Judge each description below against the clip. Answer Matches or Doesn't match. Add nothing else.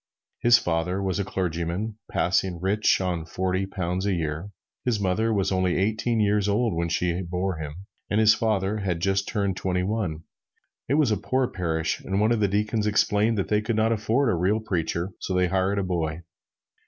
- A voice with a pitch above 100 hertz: Doesn't match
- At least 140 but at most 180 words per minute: Doesn't match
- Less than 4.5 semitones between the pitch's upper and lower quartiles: Matches